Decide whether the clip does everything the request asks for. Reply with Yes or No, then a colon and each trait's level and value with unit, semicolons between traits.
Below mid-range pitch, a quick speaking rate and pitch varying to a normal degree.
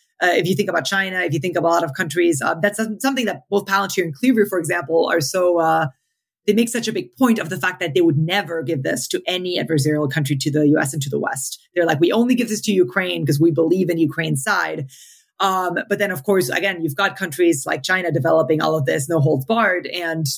No: medium, 175 Hz; fast, 255 wpm; average, 3.4 semitones